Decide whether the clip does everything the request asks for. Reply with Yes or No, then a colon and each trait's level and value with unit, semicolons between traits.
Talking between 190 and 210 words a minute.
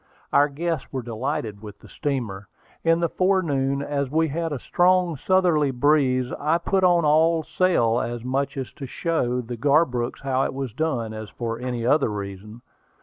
No: average, 170 wpm